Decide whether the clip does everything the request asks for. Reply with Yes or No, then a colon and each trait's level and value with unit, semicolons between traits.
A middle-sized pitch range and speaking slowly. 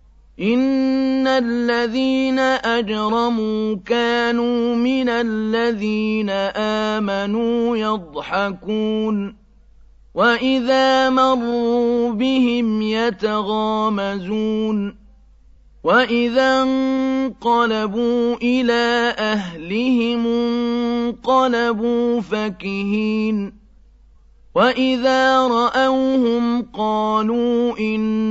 No: narrow, 1.9 semitones; slow, 50 wpm